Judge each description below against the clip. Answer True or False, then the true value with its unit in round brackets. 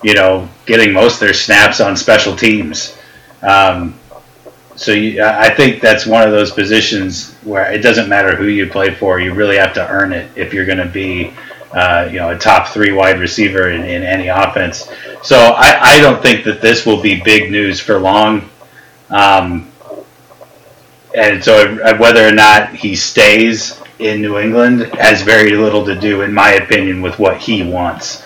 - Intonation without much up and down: True (2.1 semitones)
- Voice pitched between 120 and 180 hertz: False (105 Hz)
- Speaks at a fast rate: False (185 wpm)